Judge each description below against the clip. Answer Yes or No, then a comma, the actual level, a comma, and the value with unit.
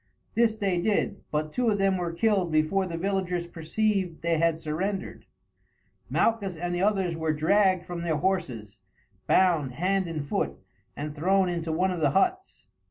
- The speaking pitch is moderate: Yes, medium, 175 Hz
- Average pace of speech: Yes, average, 165 wpm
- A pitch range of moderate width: Yes, average, 3.4 semitones